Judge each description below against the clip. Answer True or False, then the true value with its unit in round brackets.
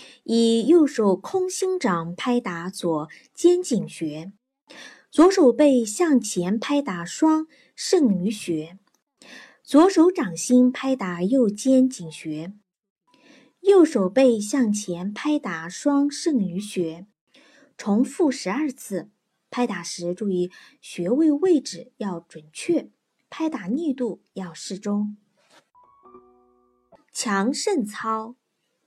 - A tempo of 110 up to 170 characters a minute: True (150 characters per minute)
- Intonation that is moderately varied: False (7.6 semitones)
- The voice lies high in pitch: True (230 Hz)